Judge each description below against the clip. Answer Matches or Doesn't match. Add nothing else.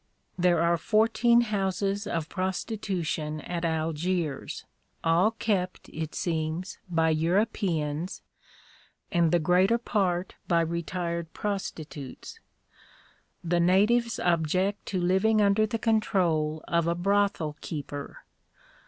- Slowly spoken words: Matches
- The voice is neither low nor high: Matches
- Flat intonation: Doesn't match